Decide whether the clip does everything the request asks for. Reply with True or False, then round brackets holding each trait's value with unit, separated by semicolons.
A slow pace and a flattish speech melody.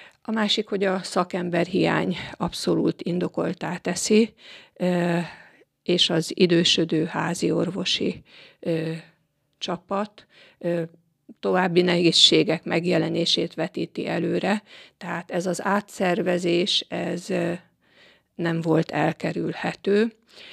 True (80 wpm; 2.2 semitones)